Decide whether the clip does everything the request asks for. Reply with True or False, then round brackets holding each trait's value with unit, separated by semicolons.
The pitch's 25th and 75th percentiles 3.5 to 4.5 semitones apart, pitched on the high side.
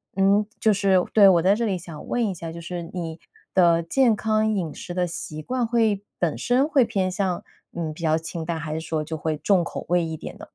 False (4.1 semitones; 180 Hz)